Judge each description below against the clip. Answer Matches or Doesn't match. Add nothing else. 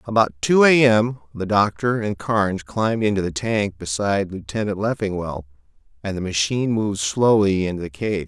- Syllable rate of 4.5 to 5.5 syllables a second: Matches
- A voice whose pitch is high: Doesn't match